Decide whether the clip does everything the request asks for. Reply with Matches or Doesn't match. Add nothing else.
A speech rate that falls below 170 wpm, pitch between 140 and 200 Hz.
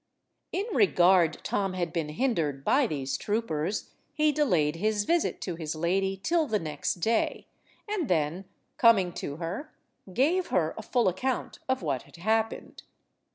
Matches